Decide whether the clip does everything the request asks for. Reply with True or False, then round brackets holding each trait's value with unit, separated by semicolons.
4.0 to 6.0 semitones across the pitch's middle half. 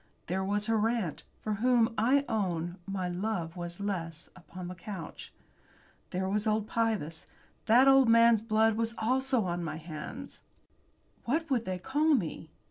True (4.6 semitones)